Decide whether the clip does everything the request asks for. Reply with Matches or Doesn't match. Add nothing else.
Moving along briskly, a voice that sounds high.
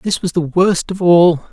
Doesn't match